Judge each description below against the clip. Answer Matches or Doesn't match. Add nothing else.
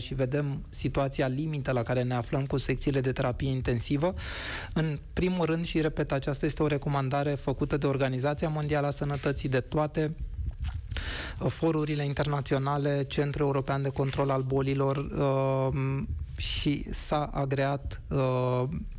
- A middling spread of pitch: Doesn't match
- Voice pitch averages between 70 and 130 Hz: Doesn't match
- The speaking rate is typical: Matches